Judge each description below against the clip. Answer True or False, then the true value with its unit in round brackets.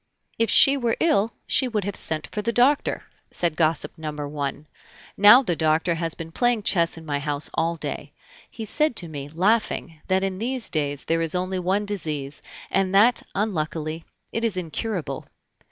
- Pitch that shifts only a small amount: False (5.6 semitones)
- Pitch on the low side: False (180 Hz)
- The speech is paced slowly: False (180 wpm)